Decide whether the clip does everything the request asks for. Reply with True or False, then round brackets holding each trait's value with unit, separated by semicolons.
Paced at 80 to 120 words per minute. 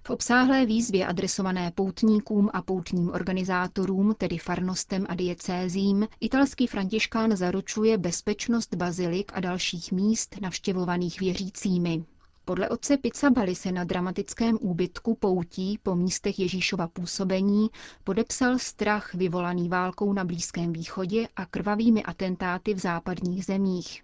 True (115 wpm)